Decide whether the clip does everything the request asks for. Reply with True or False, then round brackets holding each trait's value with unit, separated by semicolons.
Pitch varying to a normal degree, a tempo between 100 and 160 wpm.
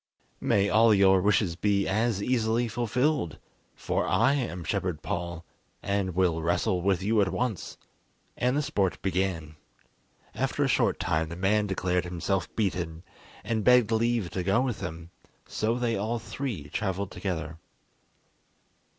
True (4.3 semitones; 145 wpm)